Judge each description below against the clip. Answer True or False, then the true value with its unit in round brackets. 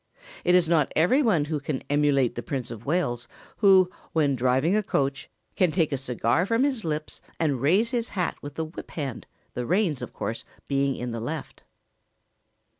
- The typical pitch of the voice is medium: True (150 Hz)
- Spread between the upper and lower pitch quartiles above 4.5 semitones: True (5.1 semitones)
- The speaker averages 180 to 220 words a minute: True (190 wpm)